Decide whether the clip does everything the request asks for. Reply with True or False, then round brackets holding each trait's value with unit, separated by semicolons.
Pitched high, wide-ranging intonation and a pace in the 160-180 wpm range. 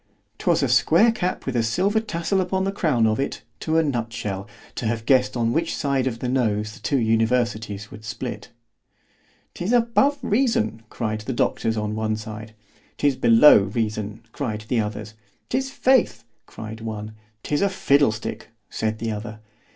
False (115 Hz; 5.7 semitones; 165 wpm)